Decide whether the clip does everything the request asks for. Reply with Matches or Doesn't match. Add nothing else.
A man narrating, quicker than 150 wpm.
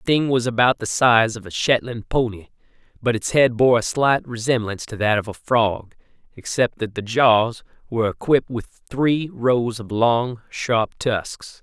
Matches